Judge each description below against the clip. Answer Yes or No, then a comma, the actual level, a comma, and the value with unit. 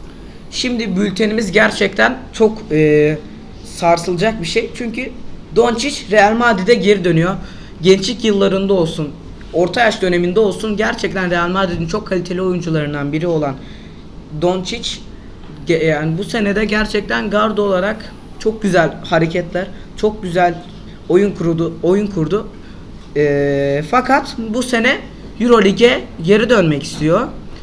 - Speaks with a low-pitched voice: No, high, 195 Hz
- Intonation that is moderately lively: Yes, average, 4.4 semitones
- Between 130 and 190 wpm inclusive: No, average, 115 wpm